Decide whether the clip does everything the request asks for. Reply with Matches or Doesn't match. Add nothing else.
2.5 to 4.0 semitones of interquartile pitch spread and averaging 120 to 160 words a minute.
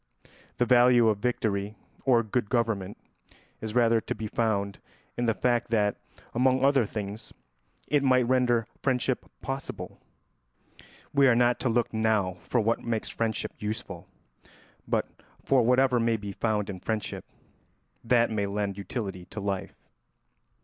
Matches